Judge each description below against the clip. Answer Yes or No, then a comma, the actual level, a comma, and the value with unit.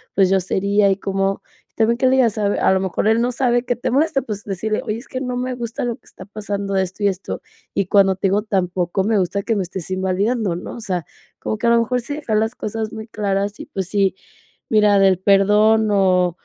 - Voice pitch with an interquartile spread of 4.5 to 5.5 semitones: No, average, 2.9 semitones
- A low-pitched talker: No, high, 205 Hz